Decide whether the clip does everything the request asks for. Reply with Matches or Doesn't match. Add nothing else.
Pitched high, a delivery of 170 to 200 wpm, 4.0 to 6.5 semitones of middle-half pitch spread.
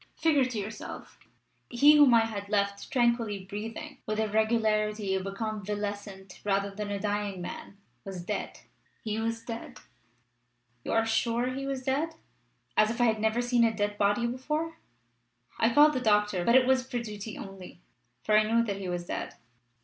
Doesn't match